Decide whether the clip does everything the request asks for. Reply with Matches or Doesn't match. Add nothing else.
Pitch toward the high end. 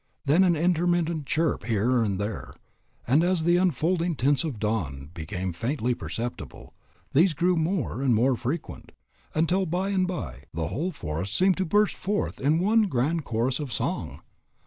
Doesn't match